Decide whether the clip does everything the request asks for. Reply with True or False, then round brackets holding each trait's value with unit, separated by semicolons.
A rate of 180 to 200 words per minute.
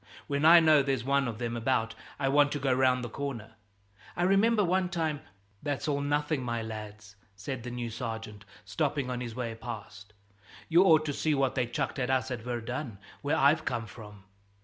True (195 wpm)